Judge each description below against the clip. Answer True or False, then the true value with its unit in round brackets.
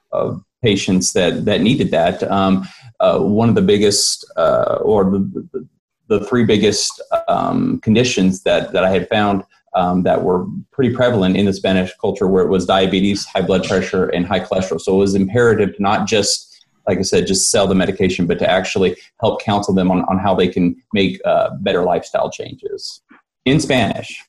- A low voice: True (100 Hz)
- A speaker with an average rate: True (190 wpm)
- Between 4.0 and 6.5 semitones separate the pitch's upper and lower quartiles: True (4.8 semitones)